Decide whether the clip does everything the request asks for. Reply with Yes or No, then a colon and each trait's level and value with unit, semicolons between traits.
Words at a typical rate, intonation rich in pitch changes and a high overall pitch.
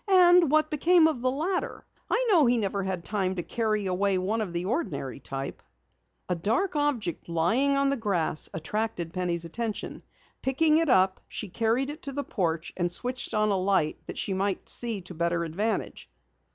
Yes: average, 185 wpm; wide, 7.3 semitones; high, 210 Hz